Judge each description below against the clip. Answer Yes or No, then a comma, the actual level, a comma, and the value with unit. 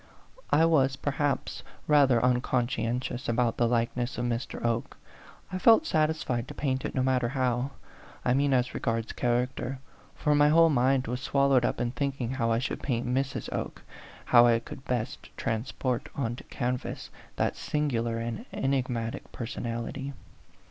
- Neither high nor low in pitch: No, low, 125 Hz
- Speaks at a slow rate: No, average, 155 wpm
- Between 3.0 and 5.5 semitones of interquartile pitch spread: No, narrow, 2.5 semitones